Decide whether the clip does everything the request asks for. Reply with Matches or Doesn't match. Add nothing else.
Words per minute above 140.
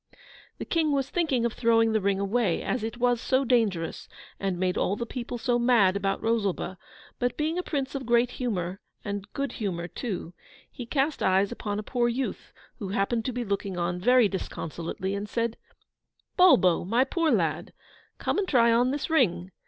Matches